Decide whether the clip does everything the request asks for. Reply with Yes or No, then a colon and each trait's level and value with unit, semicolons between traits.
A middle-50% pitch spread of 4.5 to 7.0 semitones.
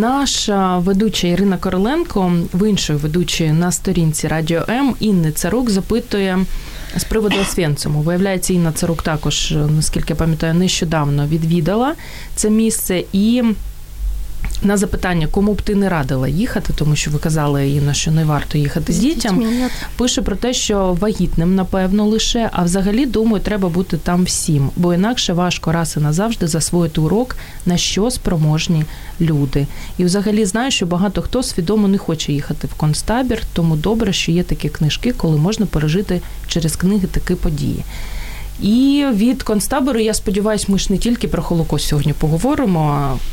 Yes: average, 4.8 semitones